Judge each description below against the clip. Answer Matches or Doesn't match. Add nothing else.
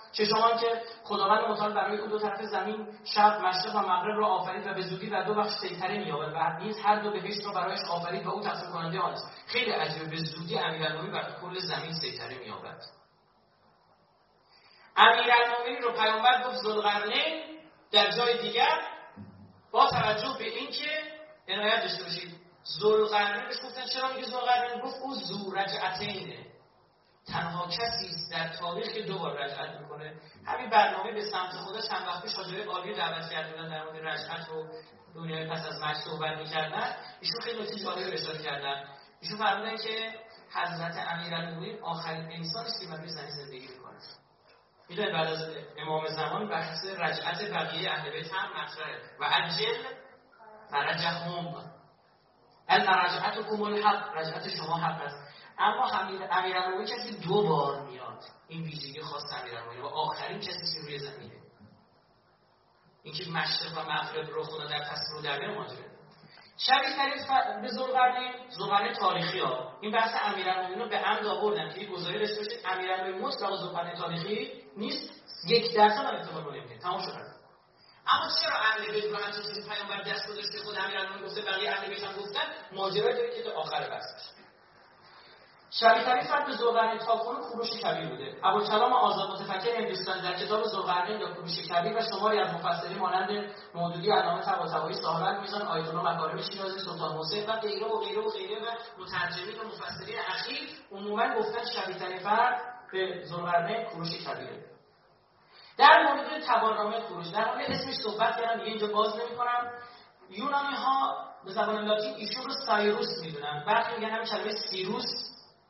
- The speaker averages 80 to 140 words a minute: Doesn't match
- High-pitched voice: Matches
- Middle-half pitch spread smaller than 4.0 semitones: Doesn't match